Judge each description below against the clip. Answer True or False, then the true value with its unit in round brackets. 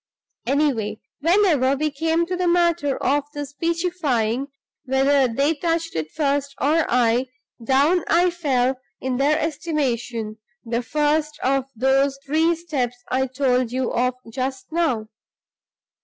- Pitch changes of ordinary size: True (4.2 semitones)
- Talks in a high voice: True (280 Hz)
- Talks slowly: True (130 wpm)